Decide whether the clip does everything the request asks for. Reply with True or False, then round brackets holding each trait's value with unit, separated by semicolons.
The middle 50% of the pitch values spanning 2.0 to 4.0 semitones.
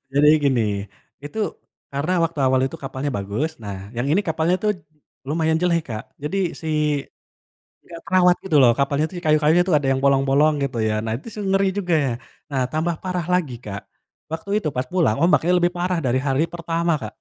False (4.5 semitones)